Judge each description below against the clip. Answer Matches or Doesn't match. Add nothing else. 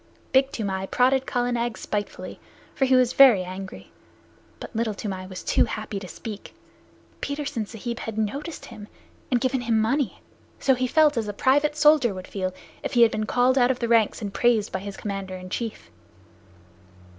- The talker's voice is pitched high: Matches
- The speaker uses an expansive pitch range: Doesn't match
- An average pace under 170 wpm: Doesn't match